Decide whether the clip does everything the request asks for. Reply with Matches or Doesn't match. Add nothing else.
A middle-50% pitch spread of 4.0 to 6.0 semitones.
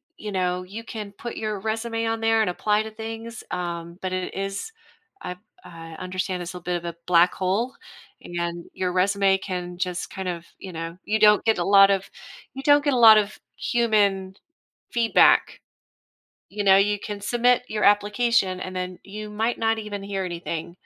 Doesn't match